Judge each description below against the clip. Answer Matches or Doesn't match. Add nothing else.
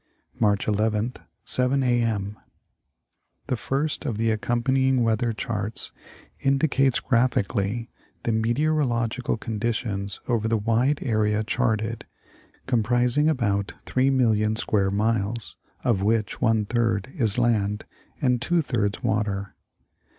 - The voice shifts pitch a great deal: Doesn't match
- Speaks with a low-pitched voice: Matches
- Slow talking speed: Matches